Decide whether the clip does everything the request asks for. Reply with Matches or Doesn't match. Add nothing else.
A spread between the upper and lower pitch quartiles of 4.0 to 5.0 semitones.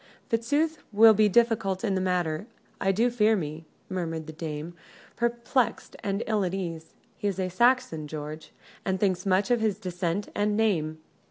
Matches